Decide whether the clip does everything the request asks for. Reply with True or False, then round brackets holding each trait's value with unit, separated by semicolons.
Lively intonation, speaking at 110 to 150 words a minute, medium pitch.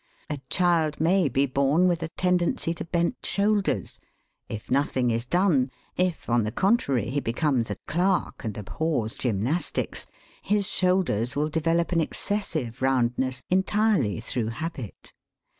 True (6.4 semitones; 140 wpm; 150 Hz)